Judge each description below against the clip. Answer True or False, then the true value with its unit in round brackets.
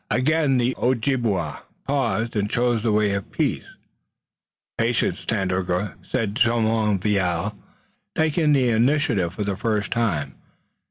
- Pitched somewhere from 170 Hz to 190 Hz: False (110 Hz)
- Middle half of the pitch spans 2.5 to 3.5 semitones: False (3.9 semitones)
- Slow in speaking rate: True (115 wpm)